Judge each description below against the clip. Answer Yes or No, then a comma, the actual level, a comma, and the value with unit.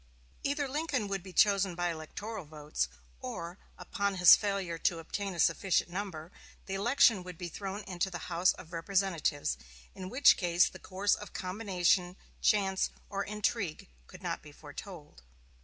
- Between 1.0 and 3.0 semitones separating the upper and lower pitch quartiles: Yes, average, 2.7 semitones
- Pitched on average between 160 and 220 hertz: Yes, high, 190 Hz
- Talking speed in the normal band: Yes, average, 155 wpm